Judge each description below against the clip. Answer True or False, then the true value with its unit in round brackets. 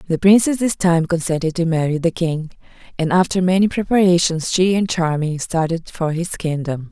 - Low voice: False (170 Hz)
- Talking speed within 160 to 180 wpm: True (175 wpm)